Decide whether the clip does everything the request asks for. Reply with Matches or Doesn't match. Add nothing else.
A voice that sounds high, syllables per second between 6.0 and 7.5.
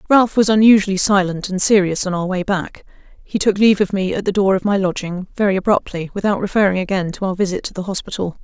Matches